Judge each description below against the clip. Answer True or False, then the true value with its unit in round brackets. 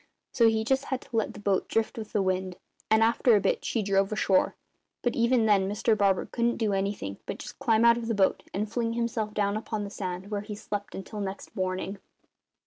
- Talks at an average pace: False (225 wpm)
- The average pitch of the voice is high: True (210 Hz)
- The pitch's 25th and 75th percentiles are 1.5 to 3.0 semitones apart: True (2.6 semitones)